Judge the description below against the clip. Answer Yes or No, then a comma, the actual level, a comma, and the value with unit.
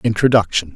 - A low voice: Yes, low, 105 Hz